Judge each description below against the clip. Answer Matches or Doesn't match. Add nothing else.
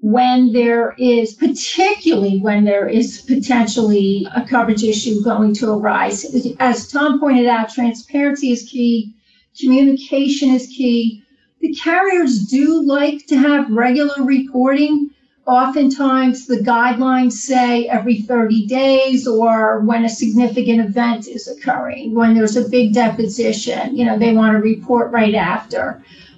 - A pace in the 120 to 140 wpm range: Matches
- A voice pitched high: Matches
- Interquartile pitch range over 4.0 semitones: Doesn't match